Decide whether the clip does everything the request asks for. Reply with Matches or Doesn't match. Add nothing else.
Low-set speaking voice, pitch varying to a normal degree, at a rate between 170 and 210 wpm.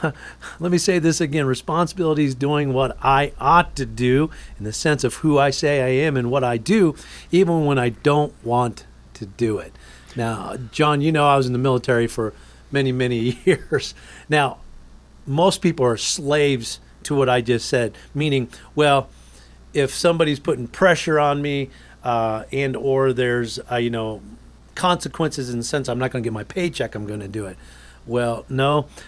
Matches